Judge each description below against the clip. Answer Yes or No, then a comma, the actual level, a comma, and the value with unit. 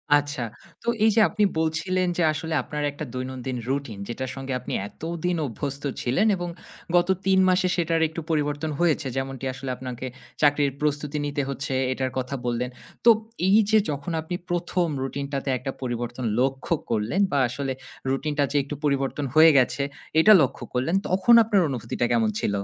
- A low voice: No, medium, 145 Hz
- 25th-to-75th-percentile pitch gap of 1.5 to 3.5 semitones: No, average, 4.0 semitones